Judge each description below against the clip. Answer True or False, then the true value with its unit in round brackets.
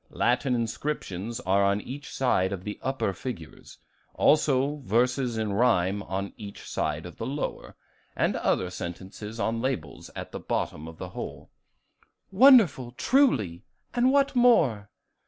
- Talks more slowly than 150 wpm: True (140 wpm)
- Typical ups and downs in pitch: False (6.1 semitones)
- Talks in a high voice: False (115 Hz)